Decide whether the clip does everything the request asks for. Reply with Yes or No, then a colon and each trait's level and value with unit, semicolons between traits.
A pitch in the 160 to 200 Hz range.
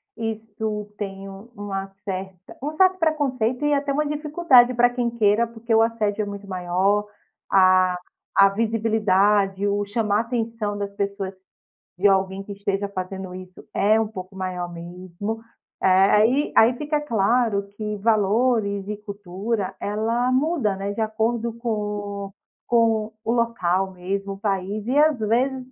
No: high, 210 Hz